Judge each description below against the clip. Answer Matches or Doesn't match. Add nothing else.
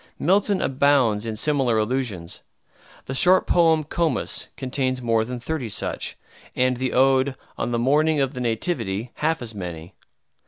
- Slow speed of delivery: Doesn't match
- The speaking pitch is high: Doesn't match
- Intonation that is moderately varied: Matches